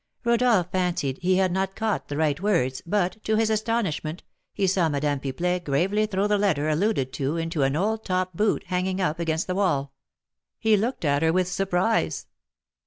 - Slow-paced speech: No, average, 180 wpm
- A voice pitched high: No, medium, 180 Hz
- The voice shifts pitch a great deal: No, average, 4.8 semitones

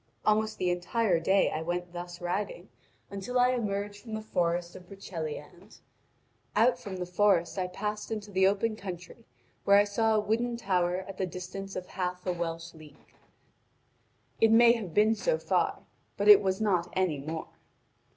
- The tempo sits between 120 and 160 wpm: No, average, 170 wpm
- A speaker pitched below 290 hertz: Yes, high, 190 Hz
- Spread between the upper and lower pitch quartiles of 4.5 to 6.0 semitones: No, average, 3.4 semitones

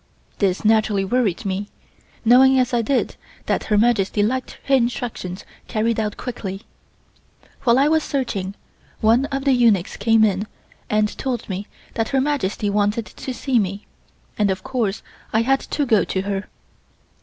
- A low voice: No, high, 225 Hz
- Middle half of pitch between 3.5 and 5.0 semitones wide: Yes, average, 3.9 semitones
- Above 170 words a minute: No, average, 160 wpm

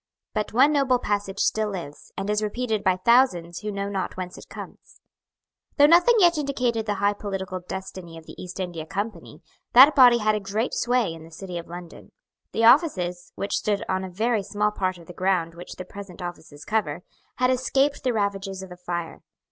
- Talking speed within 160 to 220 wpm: Yes, average, 200 wpm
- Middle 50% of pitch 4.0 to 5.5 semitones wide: Yes, average, 4.6 semitones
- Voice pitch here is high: Yes, high, 200 Hz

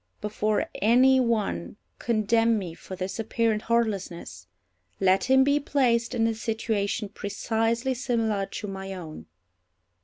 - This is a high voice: Yes, high, 220 Hz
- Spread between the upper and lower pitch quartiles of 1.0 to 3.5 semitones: Yes, average, 2.9 semitones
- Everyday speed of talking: No, slow, 125 wpm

